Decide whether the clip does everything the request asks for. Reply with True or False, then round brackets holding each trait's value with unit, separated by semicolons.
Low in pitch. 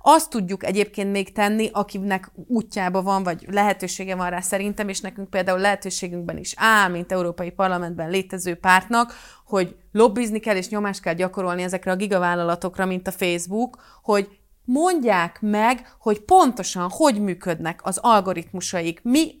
False (195 Hz)